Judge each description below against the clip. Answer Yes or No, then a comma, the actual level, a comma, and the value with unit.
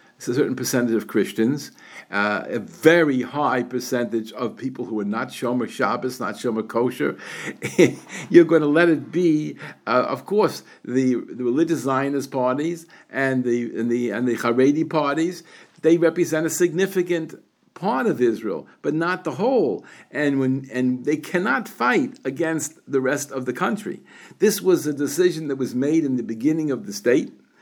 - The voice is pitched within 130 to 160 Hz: Yes, medium, 140 Hz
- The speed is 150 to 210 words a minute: Yes, average, 170 wpm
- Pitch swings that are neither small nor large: Yes, average, 4.6 semitones